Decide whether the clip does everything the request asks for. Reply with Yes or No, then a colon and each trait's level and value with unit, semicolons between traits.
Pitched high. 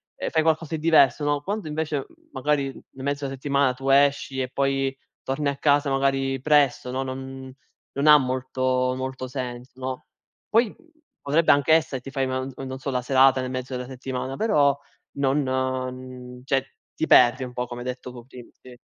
No: low, 135 Hz